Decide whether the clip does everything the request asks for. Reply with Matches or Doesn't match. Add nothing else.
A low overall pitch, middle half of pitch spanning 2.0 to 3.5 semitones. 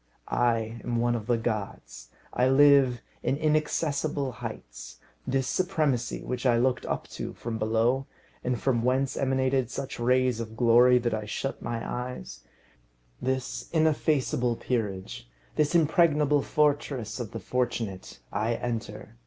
Matches